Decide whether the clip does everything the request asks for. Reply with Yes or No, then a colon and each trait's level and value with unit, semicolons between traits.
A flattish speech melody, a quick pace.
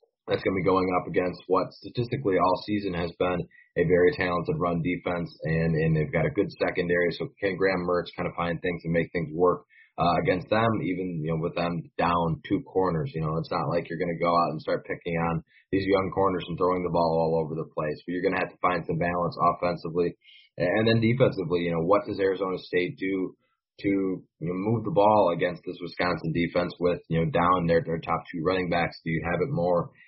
Yes: narrow, 1.7 semitones; fast, 235 wpm